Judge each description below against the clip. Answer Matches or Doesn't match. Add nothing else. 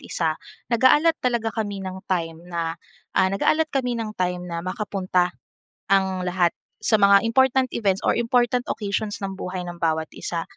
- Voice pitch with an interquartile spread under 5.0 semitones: Matches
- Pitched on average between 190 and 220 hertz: Matches